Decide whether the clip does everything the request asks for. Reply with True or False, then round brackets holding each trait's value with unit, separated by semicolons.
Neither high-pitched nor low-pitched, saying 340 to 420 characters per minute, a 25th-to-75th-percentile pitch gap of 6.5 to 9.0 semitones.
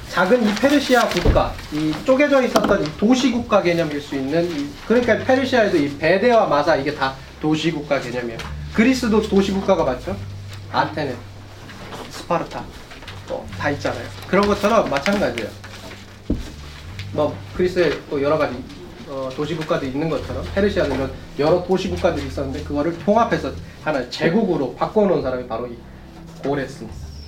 True (160 Hz; 350 characters per minute; 8.6 semitones)